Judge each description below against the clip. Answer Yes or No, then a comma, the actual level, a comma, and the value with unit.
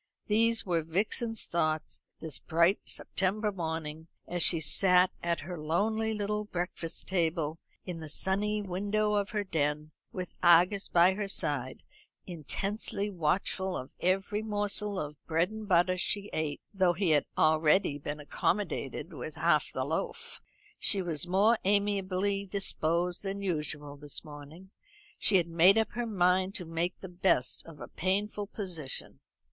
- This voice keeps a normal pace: Yes, average, 150 wpm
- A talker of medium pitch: Yes, medium, 180 Hz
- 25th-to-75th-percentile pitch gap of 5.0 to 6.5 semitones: No, average, 3.9 semitones